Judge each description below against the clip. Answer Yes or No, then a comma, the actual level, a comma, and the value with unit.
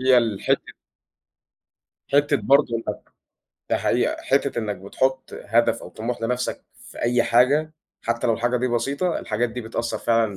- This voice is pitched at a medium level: No, low, 120 Hz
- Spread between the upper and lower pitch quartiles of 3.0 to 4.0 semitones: No, narrow, 2.4 semitones